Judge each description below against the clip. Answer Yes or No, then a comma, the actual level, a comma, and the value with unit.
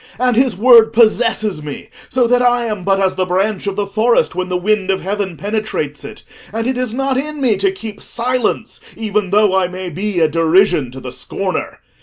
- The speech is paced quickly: Yes, fast, 210 wpm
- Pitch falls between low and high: No, high, 210 Hz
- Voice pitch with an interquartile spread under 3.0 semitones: No, average, 3.9 semitones